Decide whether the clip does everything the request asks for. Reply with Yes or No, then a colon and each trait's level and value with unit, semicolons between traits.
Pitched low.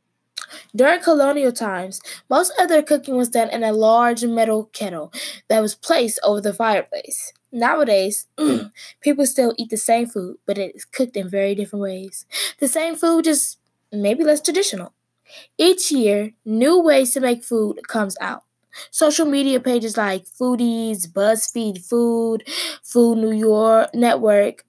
No: high, 230 Hz